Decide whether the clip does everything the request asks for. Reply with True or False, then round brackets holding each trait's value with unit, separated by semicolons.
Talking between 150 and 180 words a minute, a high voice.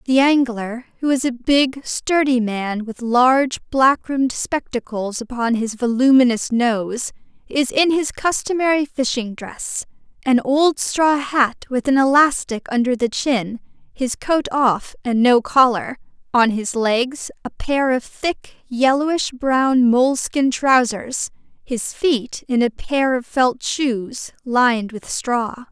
False (140 wpm; 255 Hz)